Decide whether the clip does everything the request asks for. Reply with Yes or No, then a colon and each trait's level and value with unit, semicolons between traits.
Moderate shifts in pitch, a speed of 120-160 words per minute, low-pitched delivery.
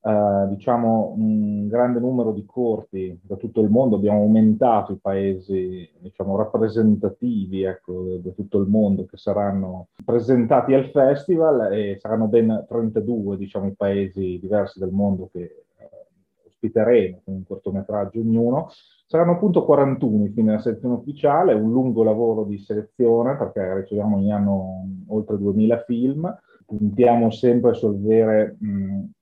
Yes: average, 3.3 semitones; average, 140 wpm; low, 110 Hz